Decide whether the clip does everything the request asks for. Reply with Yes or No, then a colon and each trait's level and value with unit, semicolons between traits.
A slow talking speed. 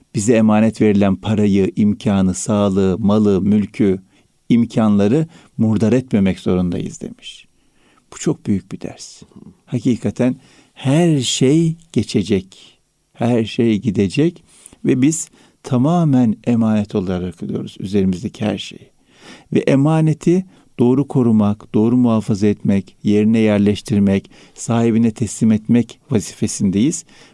No: average, 105 wpm